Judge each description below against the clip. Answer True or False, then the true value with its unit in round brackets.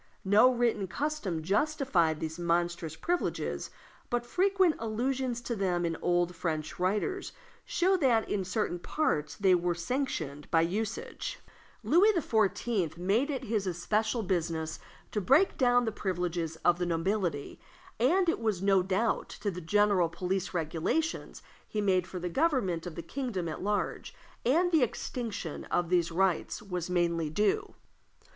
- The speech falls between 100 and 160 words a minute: True (150 wpm)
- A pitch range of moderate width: False (6.0 semitones)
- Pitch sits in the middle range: False (195 Hz)